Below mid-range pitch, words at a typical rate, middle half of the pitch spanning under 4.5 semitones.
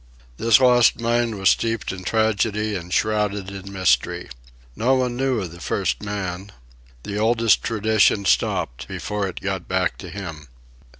Yes: low, 105 Hz; average, 155 wpm; average, 3.1 semitones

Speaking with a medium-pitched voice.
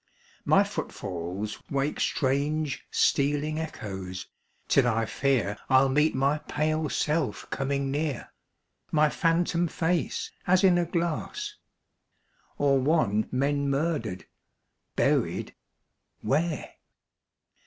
Yes: medium, 145 Hz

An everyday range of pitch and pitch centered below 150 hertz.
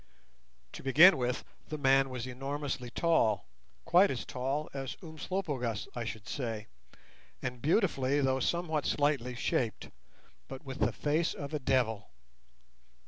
Yes: average, 3.4 semitones; low, 135 Hz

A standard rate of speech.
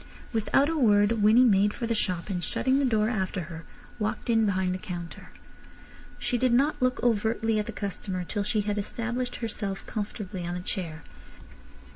Yes: average, 180 wpm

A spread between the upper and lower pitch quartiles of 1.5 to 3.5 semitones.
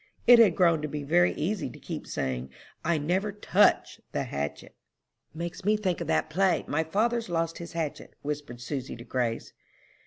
No: average, 4.8 semitones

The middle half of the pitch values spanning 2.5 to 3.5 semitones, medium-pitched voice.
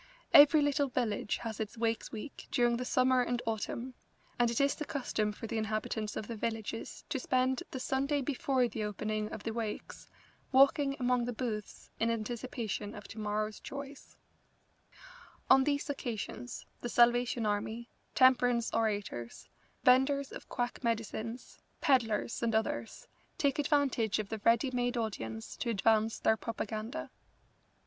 No: average, 3.0 semitones; high, 235 Hz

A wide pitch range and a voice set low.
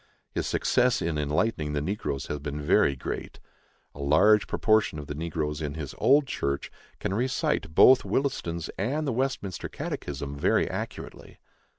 Yes: wide, 7.4 semitones; very low, 80 Hz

